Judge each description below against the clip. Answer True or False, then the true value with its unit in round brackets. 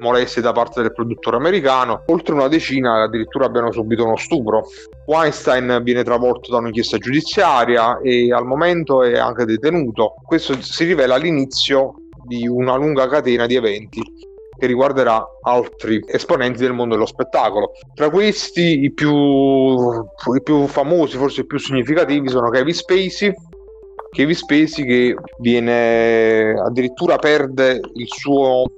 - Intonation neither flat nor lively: True (3.8 semitones)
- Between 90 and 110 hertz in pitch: False (130 Hz)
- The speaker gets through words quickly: False (140 wpm)